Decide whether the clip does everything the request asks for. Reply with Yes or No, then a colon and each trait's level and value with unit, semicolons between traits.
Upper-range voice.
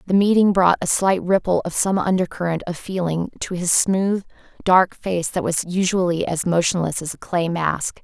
No: medium, 180 Hz